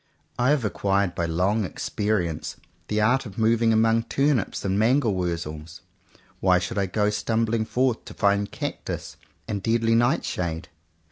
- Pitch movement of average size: Yes, average, 3.6 semitones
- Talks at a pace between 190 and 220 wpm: No, average, 150 wpm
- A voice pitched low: Yes, low, 105 Hz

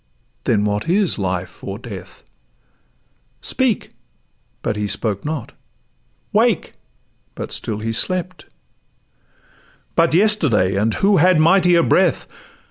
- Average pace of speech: No, slow, 110 wpm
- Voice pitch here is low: No, medium, 150 Hz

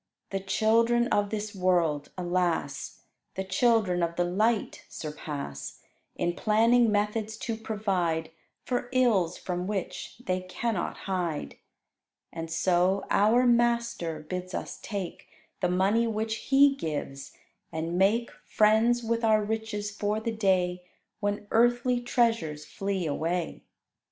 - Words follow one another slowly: Yes, slow, 125 wpm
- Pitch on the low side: No, high, 205 Hz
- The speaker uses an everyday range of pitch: Yes, average, 4.3 semitones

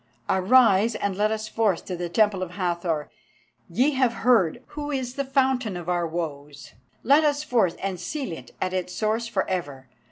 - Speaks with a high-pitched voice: Yes, high, 200 Hz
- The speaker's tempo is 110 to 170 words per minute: No, average, 190 wpm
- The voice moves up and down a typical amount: No, wide, 6.1 semitones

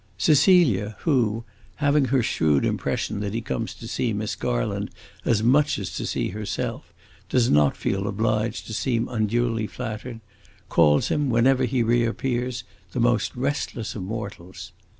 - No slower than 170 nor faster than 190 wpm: No, average, 150 wpm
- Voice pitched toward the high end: No, low, 115 Hz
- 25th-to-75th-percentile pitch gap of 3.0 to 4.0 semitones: Yes, average, 3.3 semitones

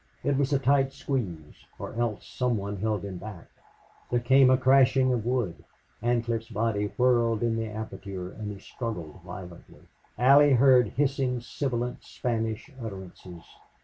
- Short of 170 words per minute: Yes, average, 145 wpm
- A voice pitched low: Yes, low, 115 Hz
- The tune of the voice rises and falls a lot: No, average, 3.9 semitones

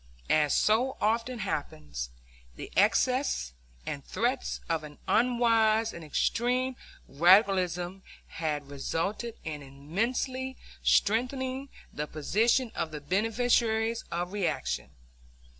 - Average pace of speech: No, slow, 100 wpm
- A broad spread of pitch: Yes, wide, 7.5 semitones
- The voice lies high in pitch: Yes, high, 210 Hz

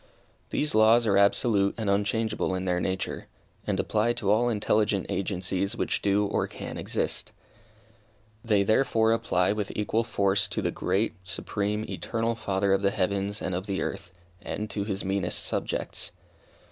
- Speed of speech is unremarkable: Yes, average, 160 wpm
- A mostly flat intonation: Yes, narrow, 2.0 semitones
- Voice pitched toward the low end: Yes, low, 100 Hz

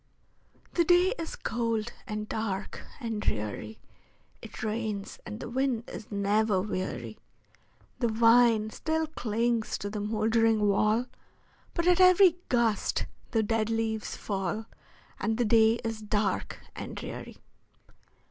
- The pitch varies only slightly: Yes, narrow, 2.1 semitones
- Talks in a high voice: Yes, high, 220 Hz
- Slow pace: Yes, slow, 130 wpm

